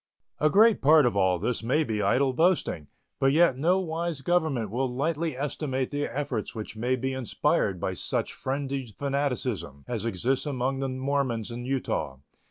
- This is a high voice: No, low, 135 Hz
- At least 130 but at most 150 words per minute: No, average, 170 wpm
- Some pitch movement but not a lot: Yes, average, 3.6 semitones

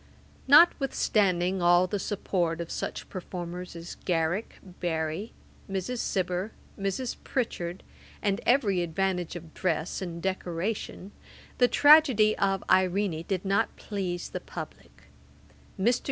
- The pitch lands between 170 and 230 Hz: Yes, medium, 185 Hz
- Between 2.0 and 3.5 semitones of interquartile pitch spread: Yes, average, 2.9 semitones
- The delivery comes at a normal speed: No, slow, 115 wpm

